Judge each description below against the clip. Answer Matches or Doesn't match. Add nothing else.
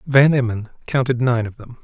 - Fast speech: Doesn't match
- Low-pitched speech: Matches